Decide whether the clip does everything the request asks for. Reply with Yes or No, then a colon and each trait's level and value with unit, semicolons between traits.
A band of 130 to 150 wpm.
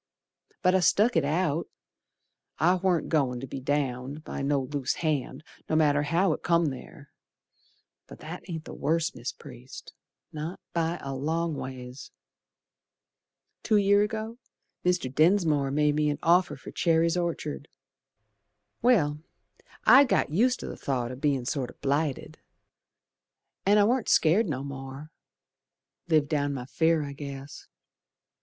Yes: average, 145 wpm